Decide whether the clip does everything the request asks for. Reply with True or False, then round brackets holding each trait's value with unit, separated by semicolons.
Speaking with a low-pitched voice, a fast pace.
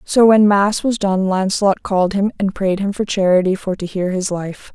False (195 Hz; 230 wpm)